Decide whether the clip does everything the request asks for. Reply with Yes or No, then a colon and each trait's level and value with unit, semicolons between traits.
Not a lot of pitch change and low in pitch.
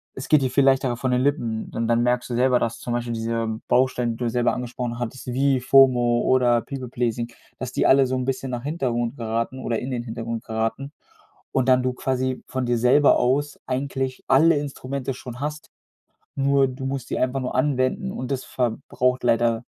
Yes: narrow, 1.9 semitones; low, 125 Hz